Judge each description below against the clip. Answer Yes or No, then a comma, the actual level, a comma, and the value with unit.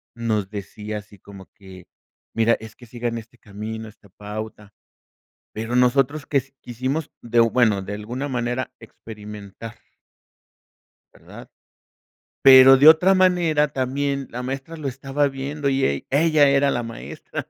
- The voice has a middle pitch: No, low, 120 Hz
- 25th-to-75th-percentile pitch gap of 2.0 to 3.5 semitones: No, average, 4.2 semitones